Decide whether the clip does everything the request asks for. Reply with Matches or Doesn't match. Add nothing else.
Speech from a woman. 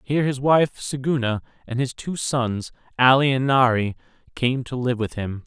Doesn't match